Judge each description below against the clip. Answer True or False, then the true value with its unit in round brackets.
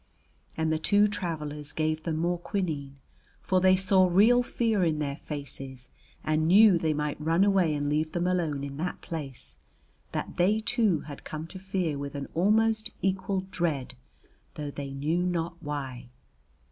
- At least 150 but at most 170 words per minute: True (165 wpm)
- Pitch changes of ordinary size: True (4.2 semitones)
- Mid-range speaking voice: True (165 Hz)